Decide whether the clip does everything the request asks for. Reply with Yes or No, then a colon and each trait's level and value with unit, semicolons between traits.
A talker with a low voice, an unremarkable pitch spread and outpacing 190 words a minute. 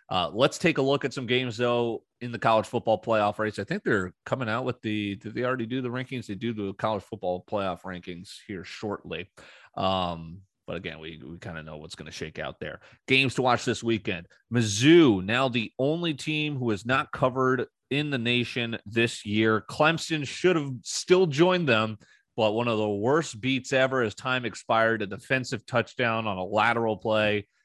Yes: low, 115 Hz; average, 3.6 semitones; average, 200 wpm